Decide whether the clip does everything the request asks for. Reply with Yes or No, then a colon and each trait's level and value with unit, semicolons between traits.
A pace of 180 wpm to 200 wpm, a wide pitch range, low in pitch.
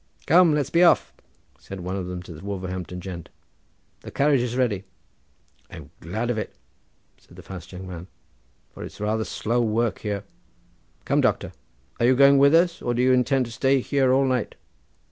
Yes: average, 185 wpm; wide, 6.1 semitones; low, 115 Hz